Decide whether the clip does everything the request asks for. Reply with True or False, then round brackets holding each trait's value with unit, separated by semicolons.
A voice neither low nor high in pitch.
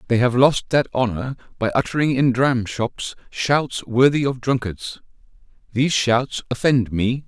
False (125 Hz)